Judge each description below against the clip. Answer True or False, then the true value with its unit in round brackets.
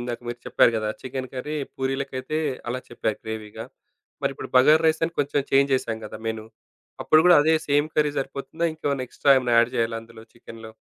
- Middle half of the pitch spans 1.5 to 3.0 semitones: False (3.9 semitones)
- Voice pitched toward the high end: False (130 Hz)